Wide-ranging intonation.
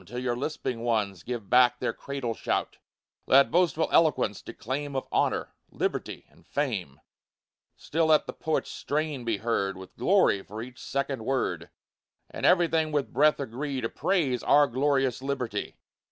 No: average, 4.1 semitones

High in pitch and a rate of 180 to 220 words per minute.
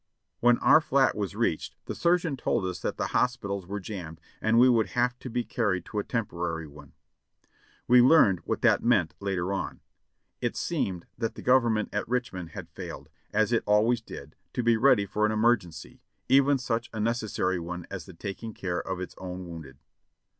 No: low, 105 Hz; average, 195 wpm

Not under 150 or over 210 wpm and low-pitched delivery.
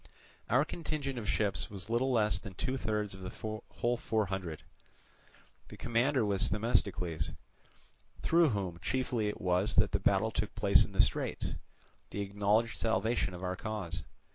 Yes: average, 160 wpm; low, 105 Hz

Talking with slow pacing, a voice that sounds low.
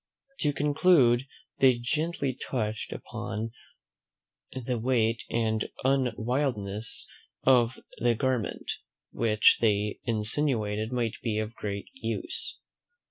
Yes: slow, 95 wpm; low, 120 Hz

